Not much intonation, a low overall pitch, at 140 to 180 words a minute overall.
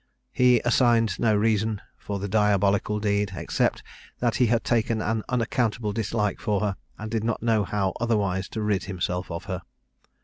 Yes: narrow, 2.2 semitones; low, 105 Hz; average, 170 wpm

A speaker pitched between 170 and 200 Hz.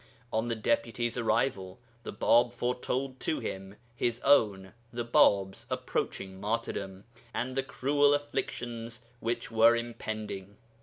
No: low, 115 Hz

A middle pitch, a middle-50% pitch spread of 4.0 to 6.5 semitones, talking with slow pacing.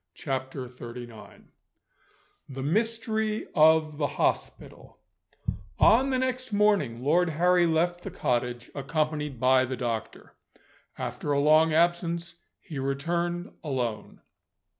Yes: medium, 155 Hz; average, 4.9 semitones; slow, 110 wpm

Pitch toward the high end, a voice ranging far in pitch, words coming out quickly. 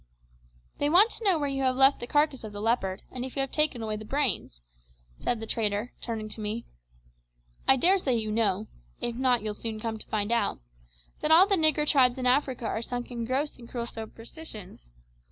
No: high, 245 Hz; average, 4.2 semitones; fast, 210 wpm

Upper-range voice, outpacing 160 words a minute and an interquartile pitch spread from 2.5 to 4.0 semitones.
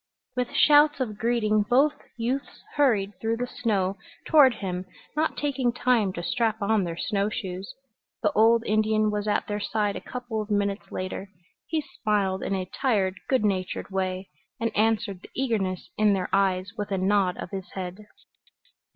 Yes: high, 210 Hz; average, 170 wpm; average, 3.3 semitones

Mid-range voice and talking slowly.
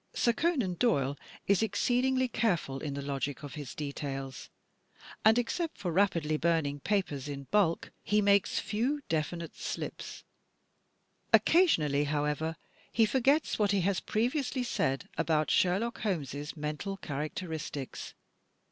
Yes: medium, 175 Hz; slow, 125 wpm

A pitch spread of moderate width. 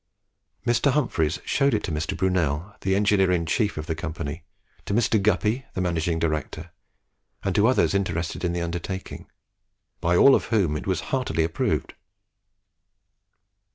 Yes: average, 4.1 semitones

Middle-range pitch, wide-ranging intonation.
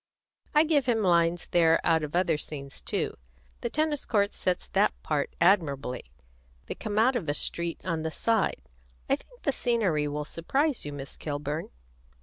Yes: medium, 170 Hz; wide, 7.3 semitones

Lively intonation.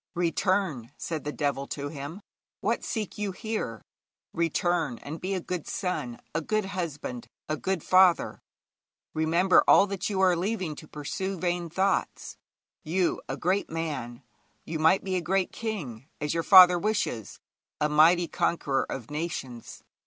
No: average, 4.2 semitones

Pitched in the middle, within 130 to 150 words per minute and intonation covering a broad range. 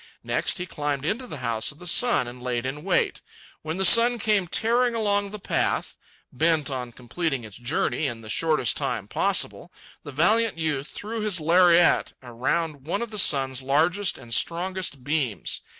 No: medium, 160 Hz; average, 175 wpm; wide, 6.9 semitones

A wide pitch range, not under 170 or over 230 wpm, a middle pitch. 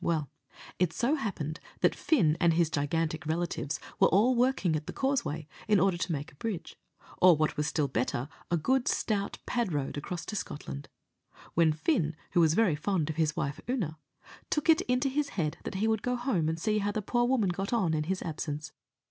Yes: wide, 6.3 semitones; fast, 205 wpm; medium, 175 Hz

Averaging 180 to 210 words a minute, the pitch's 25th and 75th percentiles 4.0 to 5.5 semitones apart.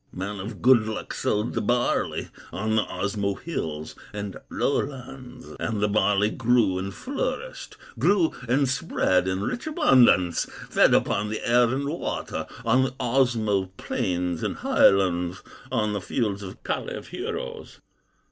No: average, 140 wpm; average, 4.7 semitones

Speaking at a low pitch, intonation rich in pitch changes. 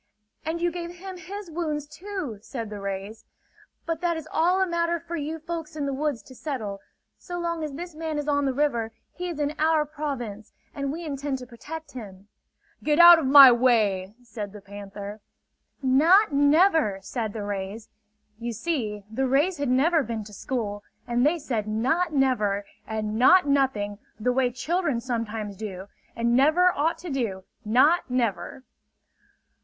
No: very high, 270 Hz; wide, 6.6 semitones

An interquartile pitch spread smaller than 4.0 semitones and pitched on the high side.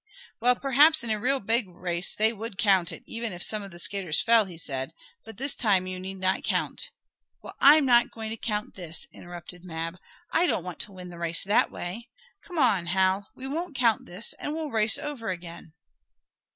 No: average, 4.9 semitones; high, 205 Hz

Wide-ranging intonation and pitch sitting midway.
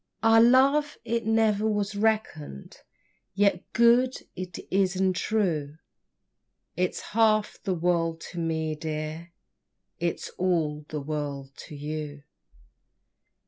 Yes: wide, 5.9 semitones; medium, 180 Hz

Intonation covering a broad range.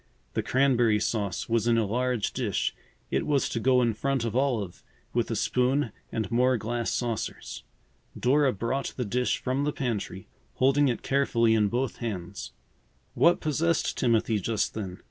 No: average, 3.2 semitones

